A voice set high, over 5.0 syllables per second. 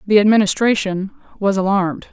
Yes: high, 200 Hz; 5.5 syllables/s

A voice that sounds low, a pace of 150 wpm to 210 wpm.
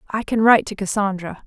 No: high, 205 Hz; fast, 205 wpm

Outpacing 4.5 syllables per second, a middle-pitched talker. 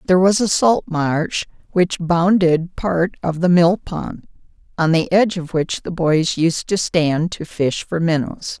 No: 4.0 syllables/s; medium, 170 Hz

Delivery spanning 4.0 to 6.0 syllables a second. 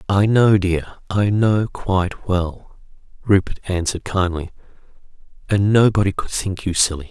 Yes: 4.6 syllables/s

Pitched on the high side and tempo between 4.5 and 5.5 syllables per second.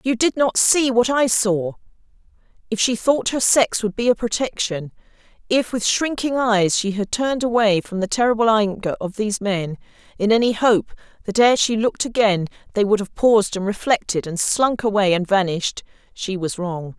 Yes: high, 215 Hz; 5.1 syllables/s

